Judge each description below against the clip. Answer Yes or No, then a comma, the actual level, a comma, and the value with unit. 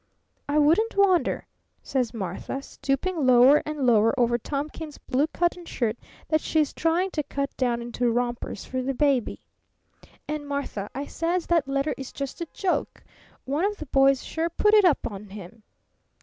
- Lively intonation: No, average, 4.8 semitones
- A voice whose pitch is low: No, very high, 280 Hz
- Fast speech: No, average, 165 wpm